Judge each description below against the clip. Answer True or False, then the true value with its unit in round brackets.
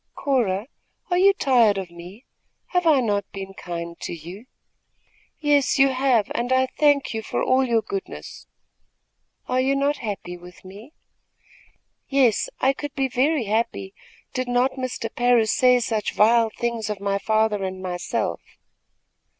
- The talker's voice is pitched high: True (235 Hz)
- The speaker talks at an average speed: True (150 wpm)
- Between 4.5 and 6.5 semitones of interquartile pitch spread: True (4.8 semitones)